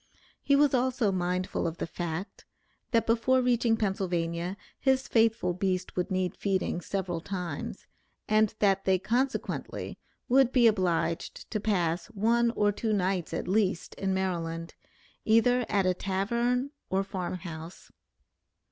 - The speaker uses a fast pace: No, average, 140 wpm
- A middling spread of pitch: Yes, average, 4.3 semitones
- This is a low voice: No, high, 195 Hz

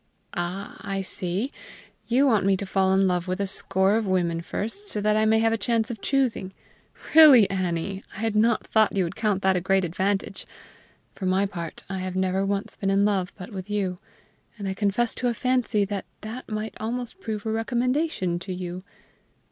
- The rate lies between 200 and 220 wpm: Yes, fast, 205 wpm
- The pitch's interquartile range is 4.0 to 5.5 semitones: No, average, 2.9 semitones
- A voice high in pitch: Yes, high, 200 Hz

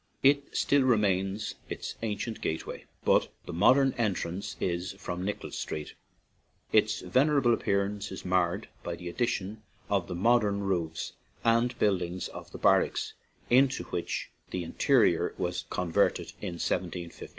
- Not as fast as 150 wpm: Yes, average, 140 wpm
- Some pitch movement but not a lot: Yes, average, 4.8 semitones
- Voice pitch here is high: No, low, 100 Hz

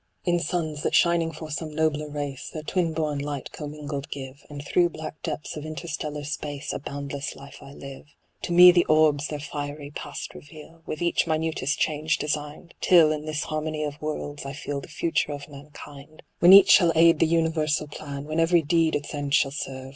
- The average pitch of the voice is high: No, medium, 150 Hz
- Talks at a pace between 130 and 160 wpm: No, average, 195 wpm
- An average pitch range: No, narrow, 1.9 semitones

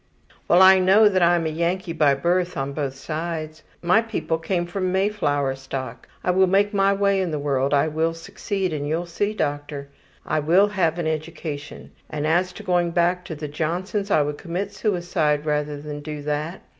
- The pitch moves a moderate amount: Yes, average, 3.9 semitones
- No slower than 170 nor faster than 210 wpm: Yes, average, 190 wpm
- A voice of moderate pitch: Yes, medium, 165 Hz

